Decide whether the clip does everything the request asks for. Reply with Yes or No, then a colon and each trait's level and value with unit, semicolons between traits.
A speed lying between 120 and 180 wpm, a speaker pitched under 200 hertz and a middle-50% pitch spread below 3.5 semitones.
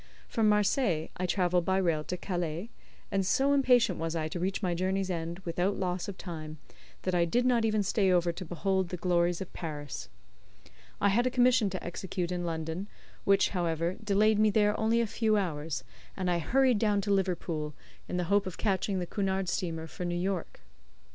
No: average, 195 wpm; medium, 185 Hz; average, 3.1 semitones